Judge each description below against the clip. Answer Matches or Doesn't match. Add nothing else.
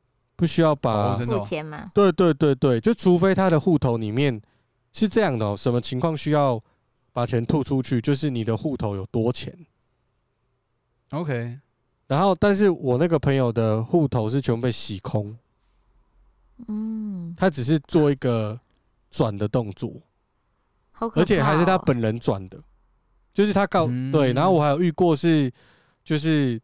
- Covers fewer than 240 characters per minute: Matches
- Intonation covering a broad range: Matches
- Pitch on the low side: Matches